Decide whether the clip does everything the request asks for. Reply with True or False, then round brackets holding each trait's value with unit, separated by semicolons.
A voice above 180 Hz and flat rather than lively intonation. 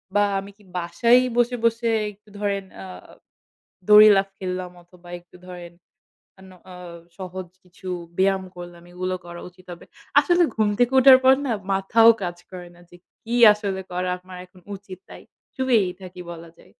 False (190 Hz; 3.0 semitones)